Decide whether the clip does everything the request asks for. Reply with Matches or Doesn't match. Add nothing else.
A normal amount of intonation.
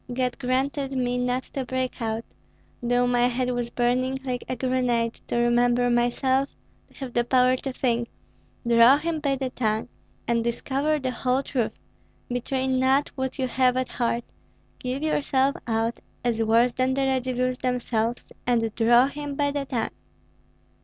Doesn't match